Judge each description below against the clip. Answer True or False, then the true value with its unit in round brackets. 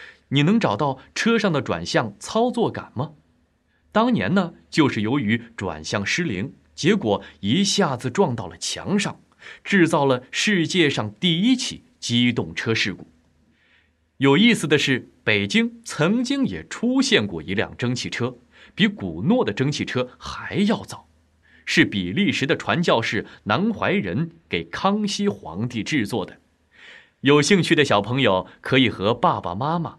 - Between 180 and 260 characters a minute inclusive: True (220 characters per minute)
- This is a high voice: False (140 Hz)